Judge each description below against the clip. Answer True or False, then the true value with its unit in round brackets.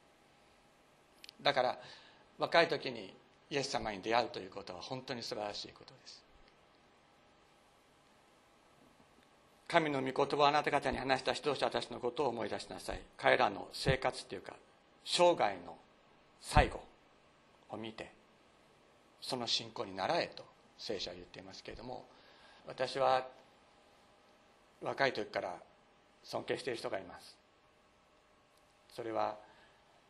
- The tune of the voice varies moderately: True (3.7 semitones)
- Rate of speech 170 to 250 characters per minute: True (245 characters per minute)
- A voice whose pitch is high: False (120 Hz)